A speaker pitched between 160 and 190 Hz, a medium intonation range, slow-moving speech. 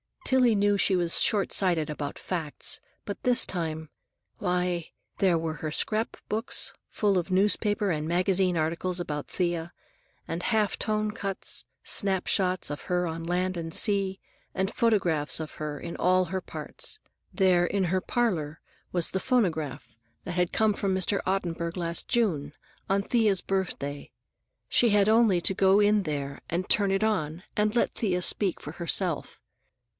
No: medium, 185 Hz; average, 3.4 semitones; average, 155 wpm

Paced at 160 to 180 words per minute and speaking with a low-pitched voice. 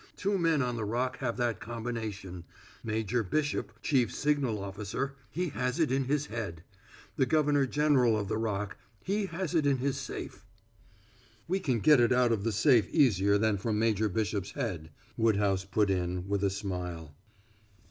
Yes: average, 170 wpm; low, 115 Hz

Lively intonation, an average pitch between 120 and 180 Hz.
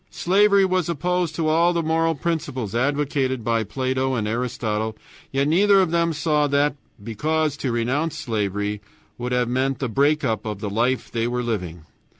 Yes: wide, 5.7 semitones; low, 135 Hz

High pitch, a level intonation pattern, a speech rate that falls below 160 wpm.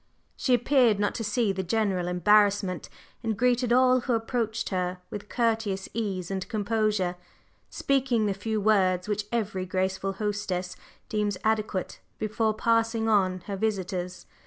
No: high, 210 Hz; average, 3.0 semitones; average, 140 wpm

